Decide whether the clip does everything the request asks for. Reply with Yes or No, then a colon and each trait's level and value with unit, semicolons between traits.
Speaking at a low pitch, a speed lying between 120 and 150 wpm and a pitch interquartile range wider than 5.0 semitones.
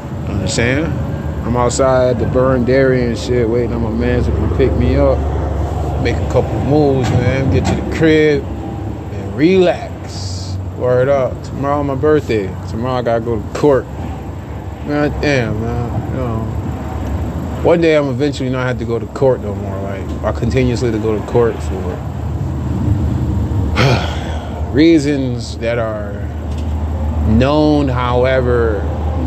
Yes: low, 110 Hz; average, 140 wpm; wide, 5.4 semitones